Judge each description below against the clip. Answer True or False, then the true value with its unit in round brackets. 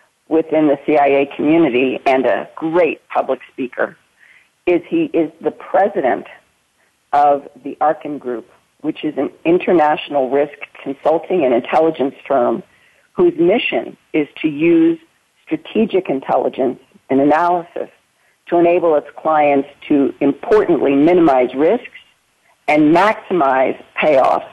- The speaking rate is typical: False (115 wpm)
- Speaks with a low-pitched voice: False (170 Hz)